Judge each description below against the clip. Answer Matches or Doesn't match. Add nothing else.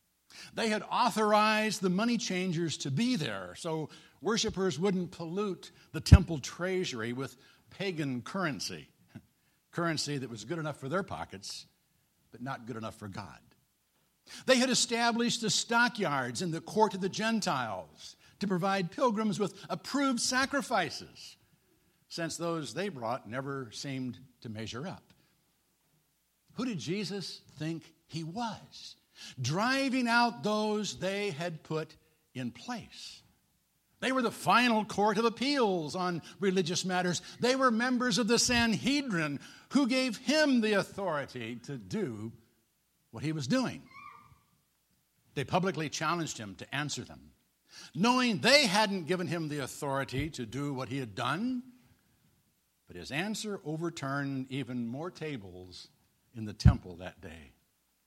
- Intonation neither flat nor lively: Doesn't match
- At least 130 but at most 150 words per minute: Matches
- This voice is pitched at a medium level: Matches